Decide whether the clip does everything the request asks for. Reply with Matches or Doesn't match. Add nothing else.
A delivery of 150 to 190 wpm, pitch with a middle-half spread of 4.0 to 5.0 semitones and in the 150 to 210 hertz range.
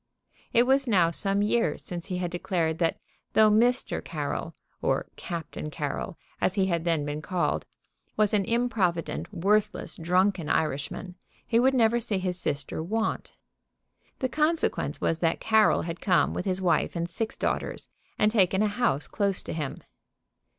Matches